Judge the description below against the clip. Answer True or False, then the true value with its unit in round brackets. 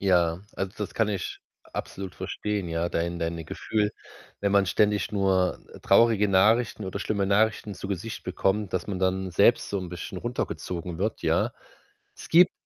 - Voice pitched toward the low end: True (95 Hz)